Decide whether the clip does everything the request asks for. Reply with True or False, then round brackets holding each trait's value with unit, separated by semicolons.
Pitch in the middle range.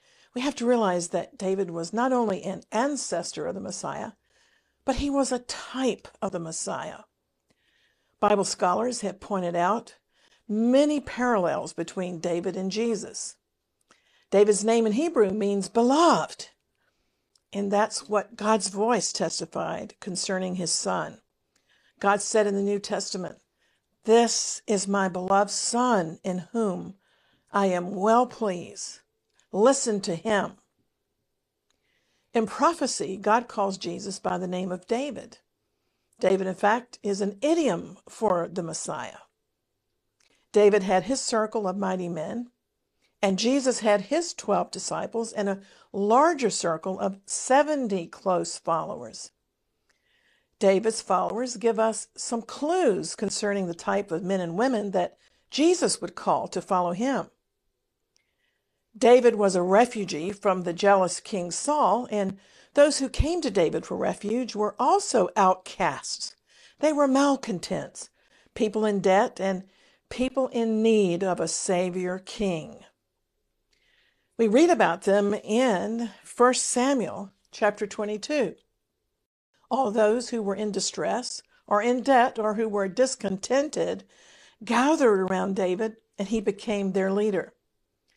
False (210 Hz)